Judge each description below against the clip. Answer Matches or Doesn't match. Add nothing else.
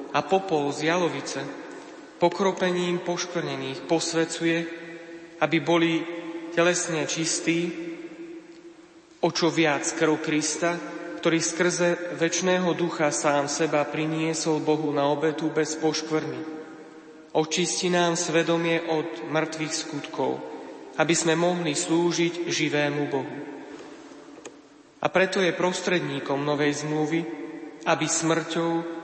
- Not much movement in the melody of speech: Matches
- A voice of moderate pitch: Matches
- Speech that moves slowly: Matches